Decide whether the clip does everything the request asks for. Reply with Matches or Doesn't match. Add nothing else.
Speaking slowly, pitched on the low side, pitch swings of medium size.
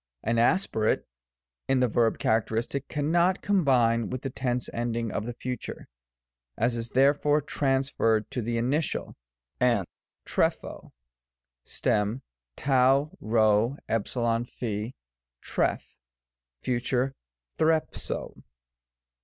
Matches